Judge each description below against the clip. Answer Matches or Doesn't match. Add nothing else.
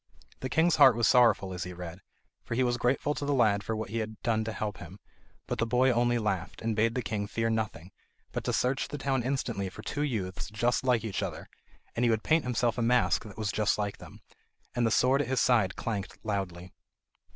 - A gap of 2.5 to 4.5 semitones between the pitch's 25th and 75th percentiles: Matches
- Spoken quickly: Matches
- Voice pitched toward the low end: Matches